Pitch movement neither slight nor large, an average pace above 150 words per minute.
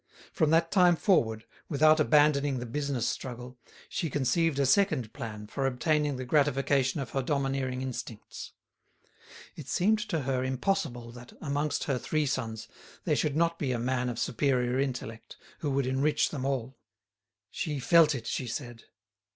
Yes: average, 3.4 semitones; average, 160 wpm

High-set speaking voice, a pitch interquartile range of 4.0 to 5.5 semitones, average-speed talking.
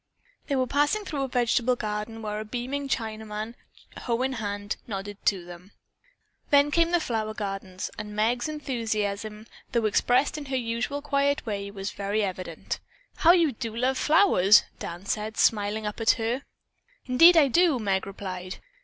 Yes: high, 225 Hz; average, 4.7 semitones; average, 160 wpm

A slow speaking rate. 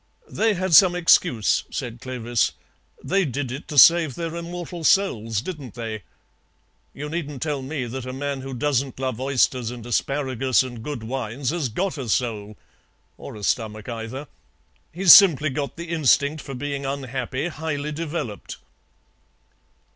No: average, 150 wpm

